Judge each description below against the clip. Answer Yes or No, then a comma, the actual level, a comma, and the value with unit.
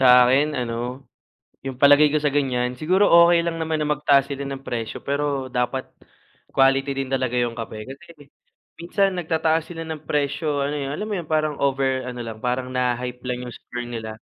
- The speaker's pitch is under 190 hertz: Yes, low, 135 Hz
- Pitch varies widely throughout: No, average, 3.4 semitones